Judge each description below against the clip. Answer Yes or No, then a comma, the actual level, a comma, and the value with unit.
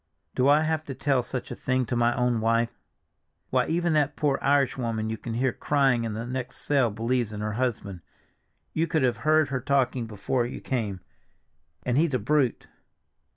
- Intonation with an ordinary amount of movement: Yes, average, 3.5 semitones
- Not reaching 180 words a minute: No, average, 190 wpm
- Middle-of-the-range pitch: No, low, 125 Hz